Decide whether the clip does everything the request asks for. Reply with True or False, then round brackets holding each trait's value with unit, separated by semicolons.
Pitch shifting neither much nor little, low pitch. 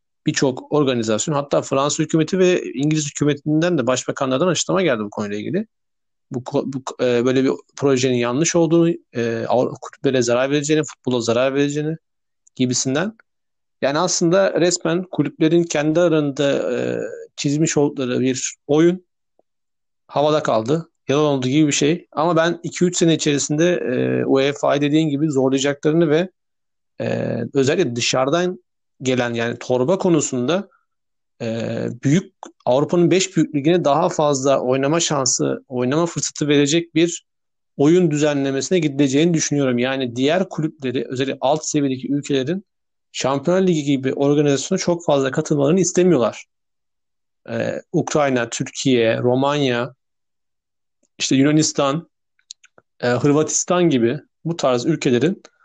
False (4.2 semitones; 145 Hz)